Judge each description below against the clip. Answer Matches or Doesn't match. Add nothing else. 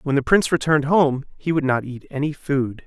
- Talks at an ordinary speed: Doesn't match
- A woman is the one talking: Doesn't match